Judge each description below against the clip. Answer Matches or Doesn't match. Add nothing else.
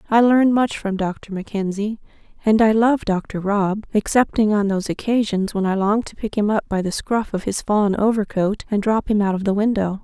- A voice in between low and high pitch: Doesn't match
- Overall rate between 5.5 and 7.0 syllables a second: Doesn't match